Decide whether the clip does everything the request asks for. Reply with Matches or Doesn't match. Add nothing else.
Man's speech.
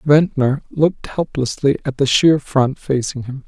Matches